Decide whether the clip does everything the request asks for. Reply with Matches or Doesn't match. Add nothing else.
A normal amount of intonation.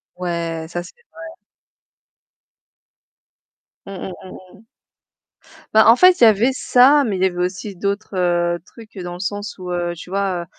Matches